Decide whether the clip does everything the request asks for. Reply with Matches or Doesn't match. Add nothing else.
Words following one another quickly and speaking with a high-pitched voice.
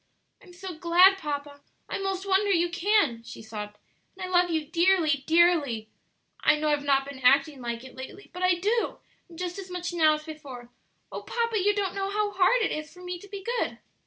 Matches